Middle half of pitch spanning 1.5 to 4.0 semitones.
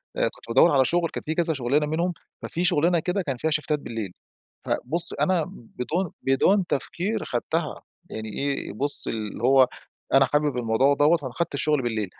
No: average, 5.2 semitones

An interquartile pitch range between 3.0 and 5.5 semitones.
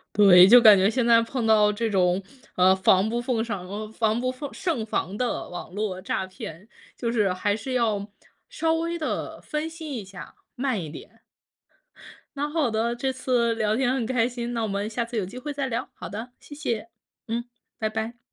Yes: average, 3.6 semitones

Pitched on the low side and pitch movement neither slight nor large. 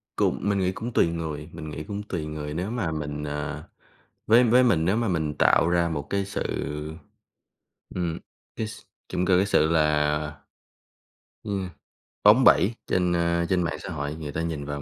Yes: very low, 85 Hz; average, 4.3 semitones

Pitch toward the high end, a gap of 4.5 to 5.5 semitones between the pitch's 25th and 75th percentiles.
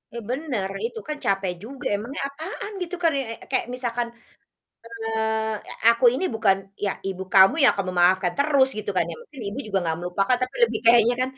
Yes: high, 230 Hz; average, 5.2 semitones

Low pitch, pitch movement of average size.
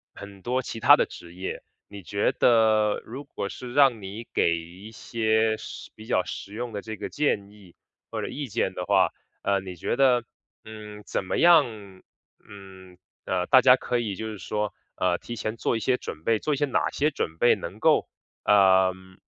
Yes: low, 105 Hz; average, 3.9 semitones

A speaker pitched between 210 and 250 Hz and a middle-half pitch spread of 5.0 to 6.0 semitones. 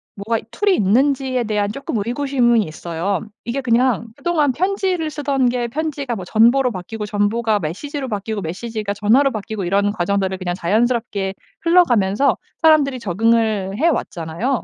Yes: high, 230 Hz; average, 5.3 semitones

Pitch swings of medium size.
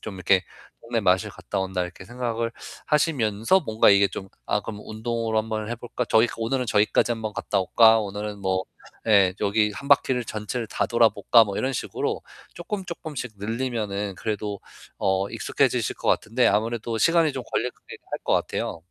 Yes: average, 3.0 semitones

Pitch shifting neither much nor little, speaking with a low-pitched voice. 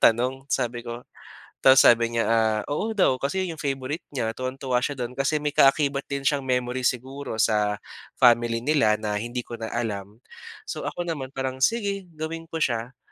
Yes: average, 3.4 semitones; low, 130 Hz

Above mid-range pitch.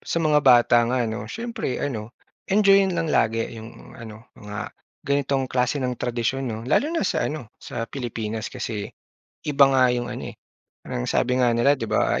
No: low, 125 Hz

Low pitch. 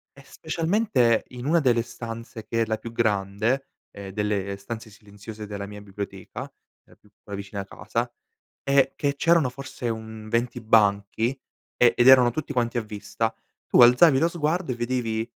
Yes: low, 115 Hz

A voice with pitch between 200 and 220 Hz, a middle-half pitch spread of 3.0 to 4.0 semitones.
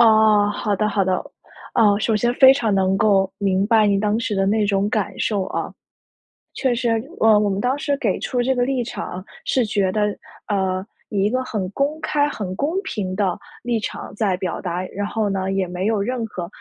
Yes: high, 210 Hz; average, 3.3 semitones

